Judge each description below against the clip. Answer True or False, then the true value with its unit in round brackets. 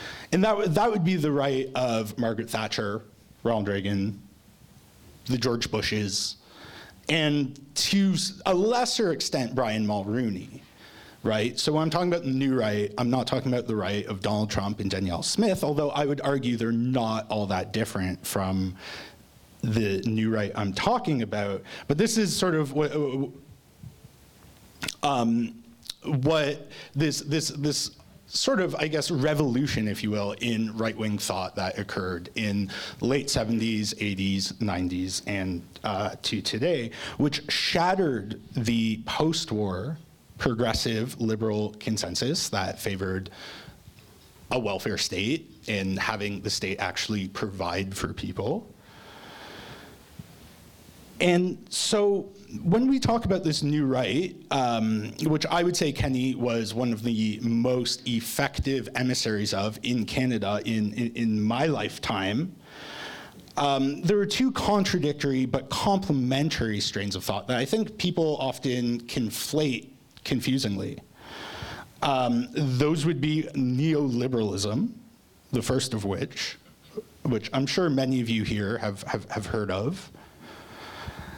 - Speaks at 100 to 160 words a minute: True (135 wpm)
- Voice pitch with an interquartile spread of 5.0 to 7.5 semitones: True (5.6 semitones)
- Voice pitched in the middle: False (120 Hz)